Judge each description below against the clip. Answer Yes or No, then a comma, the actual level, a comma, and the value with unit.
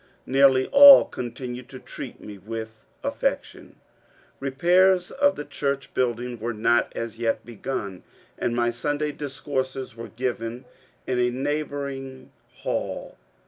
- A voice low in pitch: Yes, low, 130 Hz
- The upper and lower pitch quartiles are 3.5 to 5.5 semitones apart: No, average, 3.0 semitones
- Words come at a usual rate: No, slow, 125 wpm